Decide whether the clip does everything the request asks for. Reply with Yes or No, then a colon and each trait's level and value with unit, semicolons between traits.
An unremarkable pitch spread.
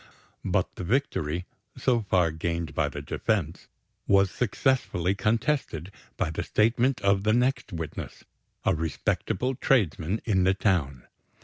No: wide, 5.7 semitones